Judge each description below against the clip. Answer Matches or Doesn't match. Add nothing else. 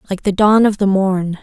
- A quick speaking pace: Matches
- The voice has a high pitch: Matches